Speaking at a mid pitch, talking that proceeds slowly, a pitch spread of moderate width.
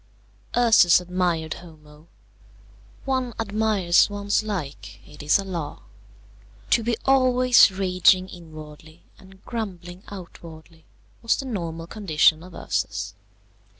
Yes: medium, 180 Hz; slow, 110 wpm; average, 5.0 semitones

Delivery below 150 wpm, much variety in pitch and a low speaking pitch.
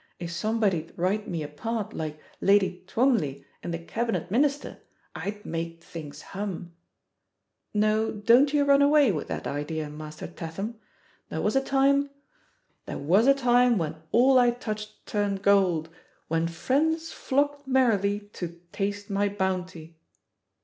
No: average, 140 wpm; wide, 6.4 semitones; high, 205 Hz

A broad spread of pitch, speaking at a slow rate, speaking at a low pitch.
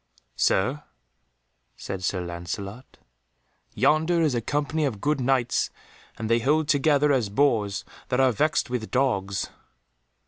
Yes: wide, 6.2 semitones; slow, 130 wpm; low, 125 Hz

